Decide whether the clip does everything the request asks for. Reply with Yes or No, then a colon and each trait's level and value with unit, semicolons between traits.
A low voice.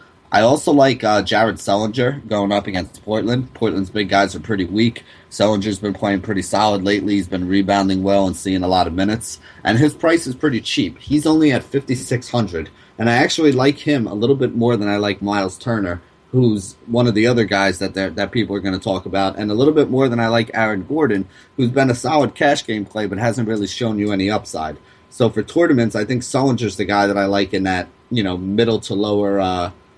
Yes: low, 105 Hz